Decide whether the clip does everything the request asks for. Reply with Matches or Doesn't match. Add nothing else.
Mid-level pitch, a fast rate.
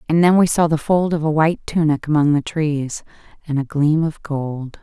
Matches